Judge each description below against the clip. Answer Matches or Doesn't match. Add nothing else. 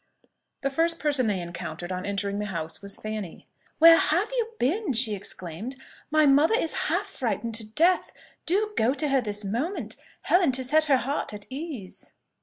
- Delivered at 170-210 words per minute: Matches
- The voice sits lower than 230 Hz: Doesn't match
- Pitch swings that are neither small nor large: Doesn't match